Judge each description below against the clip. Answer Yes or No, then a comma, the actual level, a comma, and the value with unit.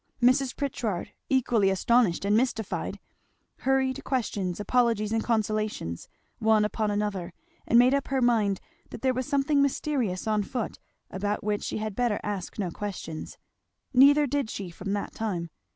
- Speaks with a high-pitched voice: Yes, high, 220 Hz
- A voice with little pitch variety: No, average, 4.0 semitones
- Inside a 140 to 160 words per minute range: Yes, average, 150 wpm